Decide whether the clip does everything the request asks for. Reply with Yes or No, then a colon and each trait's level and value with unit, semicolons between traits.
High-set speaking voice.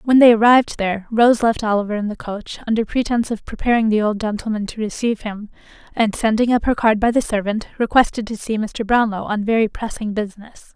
Yes: high, 220 Hz